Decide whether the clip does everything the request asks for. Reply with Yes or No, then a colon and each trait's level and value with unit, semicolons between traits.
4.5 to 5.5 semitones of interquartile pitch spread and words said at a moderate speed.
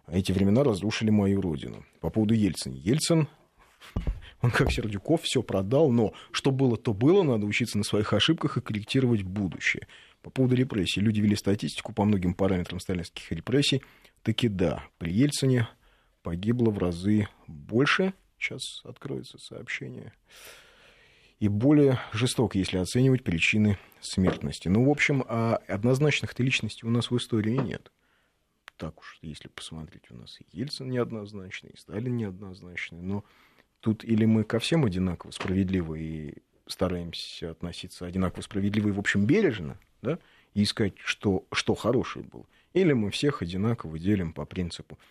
Yes: average, 5.1 semitones; average, 145 wpm